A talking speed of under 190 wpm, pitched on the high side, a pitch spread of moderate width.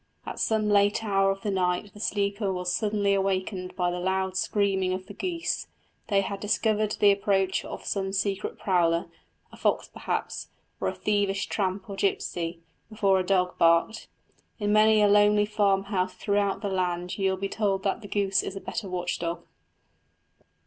No: average, 175 wpm; high, 195 Hz; narrow, 1.8 semitones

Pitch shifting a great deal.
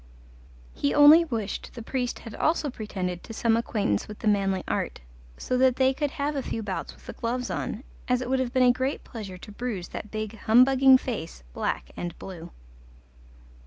No: average, 4.1 semitones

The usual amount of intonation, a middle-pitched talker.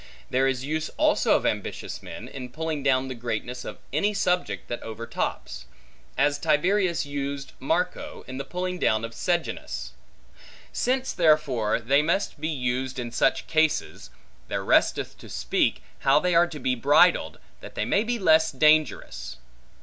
Yes: average, 4.5 semitones; medium, 145 Hz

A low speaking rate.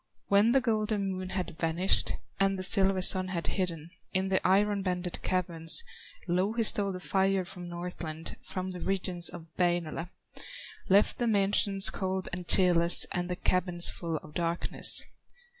No: average, 155 wpm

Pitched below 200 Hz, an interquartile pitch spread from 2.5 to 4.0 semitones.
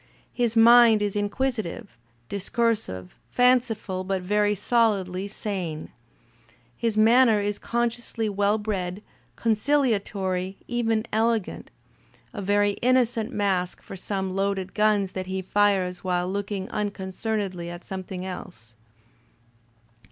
No: high, 205 Hz; average, 3.0 semitones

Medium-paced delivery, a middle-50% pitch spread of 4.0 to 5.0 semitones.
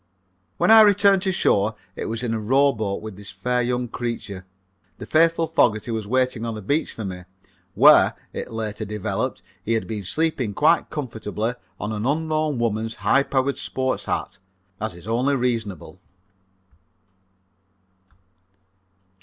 Yes: average, 145 wpm; average, 4.7 semitones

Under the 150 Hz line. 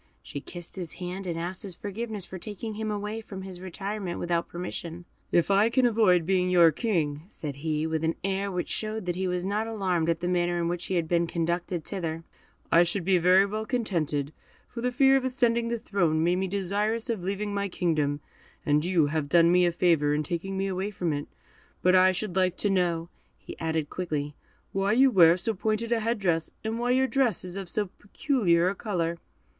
No: medium, 185 Hz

